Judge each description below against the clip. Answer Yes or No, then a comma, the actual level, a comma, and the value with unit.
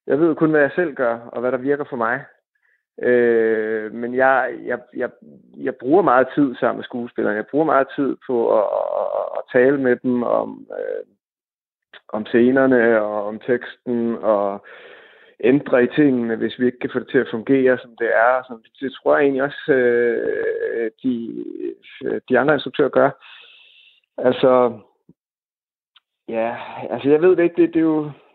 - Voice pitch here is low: Yes, low, 130 Hz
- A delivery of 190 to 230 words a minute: No, average, 170 wpm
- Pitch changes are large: Yes, wide, 7.1 semitones